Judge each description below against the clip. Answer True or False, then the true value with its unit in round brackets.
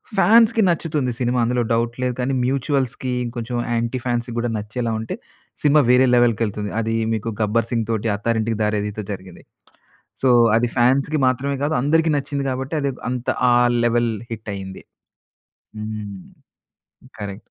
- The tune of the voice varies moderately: True (3.2 semitones)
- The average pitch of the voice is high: False (120 Hz)